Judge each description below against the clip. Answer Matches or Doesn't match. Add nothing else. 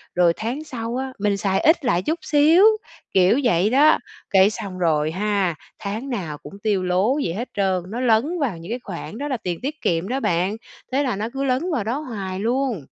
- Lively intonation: Matches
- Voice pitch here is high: Matches